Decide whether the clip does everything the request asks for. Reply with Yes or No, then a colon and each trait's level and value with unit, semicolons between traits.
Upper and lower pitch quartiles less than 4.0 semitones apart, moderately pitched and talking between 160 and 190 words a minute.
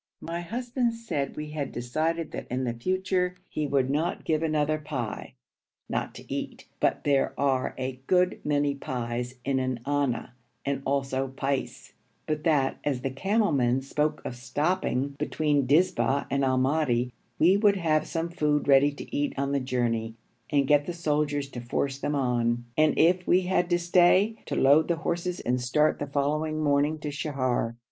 Yes: average, 3.6 semitones; medium, 145 Hz; average, 175 wpm